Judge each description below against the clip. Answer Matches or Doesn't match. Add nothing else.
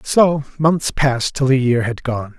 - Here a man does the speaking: Matches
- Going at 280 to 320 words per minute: Doesn't match